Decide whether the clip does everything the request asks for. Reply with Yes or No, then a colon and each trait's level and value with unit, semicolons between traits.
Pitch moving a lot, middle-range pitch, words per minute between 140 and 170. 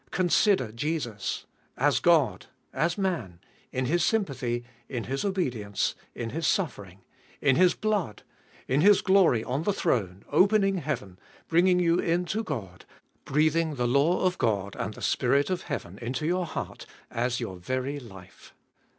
Yes: wide, 7.0 semitones; medium, 145 Hz; average, 150 wpm